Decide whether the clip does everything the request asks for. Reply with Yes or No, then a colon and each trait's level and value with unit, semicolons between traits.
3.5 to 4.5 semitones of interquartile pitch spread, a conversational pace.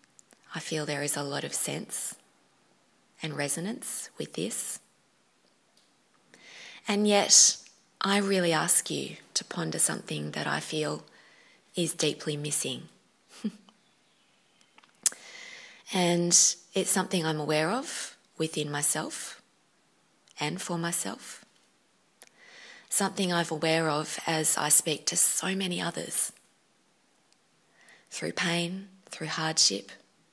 No: average, 4.0 semitones; slow, 105 wpm